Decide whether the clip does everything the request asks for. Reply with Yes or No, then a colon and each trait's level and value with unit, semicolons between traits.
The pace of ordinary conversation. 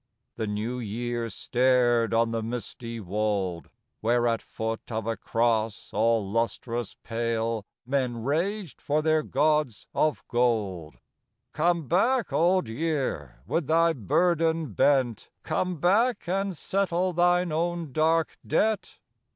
No: slow, 130 wpm